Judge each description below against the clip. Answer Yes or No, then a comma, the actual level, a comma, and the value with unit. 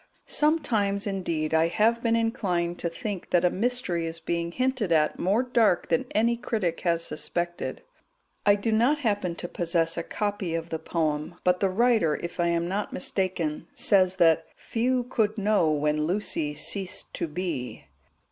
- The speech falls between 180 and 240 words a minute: No, average, 165 wpm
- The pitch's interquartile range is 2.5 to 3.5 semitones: No, average, 4.5 semitones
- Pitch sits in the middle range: Yes, medium, 180 Hz